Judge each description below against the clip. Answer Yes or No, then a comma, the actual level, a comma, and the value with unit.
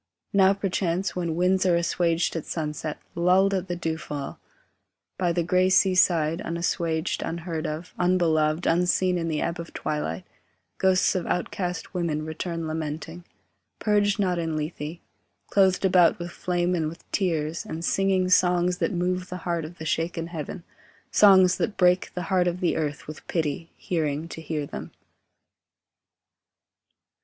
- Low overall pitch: No, medium, 175 Hz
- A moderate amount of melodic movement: No, narrow, 2.2 semitones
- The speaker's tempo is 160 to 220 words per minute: No, average, 150 wpm